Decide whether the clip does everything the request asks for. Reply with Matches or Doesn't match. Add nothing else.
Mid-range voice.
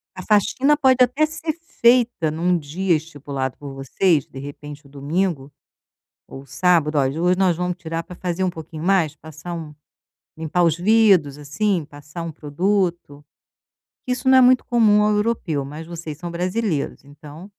Matches